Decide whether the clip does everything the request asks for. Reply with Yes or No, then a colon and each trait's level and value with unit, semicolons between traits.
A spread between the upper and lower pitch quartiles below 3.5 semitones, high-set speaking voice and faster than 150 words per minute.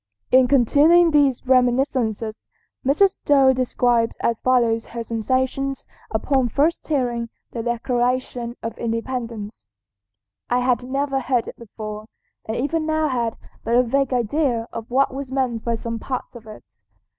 No: average, 2.8 semitones; very high, 250 Hz; average, 145 wpm